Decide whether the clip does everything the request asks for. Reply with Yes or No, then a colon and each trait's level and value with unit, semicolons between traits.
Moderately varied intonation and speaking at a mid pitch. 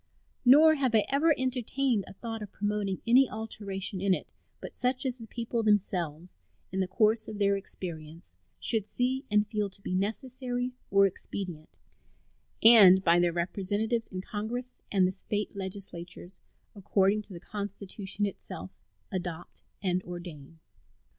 No: average, 3.7 semitones; high, 205 Hz